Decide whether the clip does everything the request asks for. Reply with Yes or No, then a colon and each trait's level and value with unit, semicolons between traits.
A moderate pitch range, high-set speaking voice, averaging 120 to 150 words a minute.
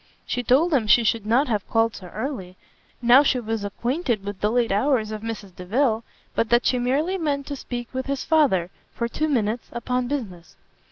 No: average, 4.1 semitones; high, 235 Hz; average, 200 wpm